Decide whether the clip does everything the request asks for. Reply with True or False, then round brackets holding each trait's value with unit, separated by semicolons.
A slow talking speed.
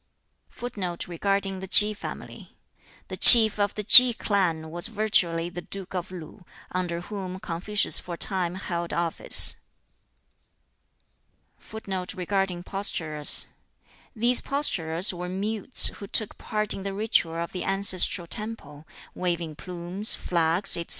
True (120 wpm)